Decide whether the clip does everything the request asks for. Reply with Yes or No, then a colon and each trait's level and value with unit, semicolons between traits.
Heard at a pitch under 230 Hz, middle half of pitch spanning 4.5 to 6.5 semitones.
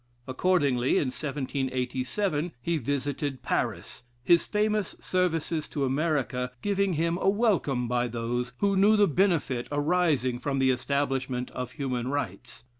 Yes: medium, 140 Hz; wide, 5.4 semitones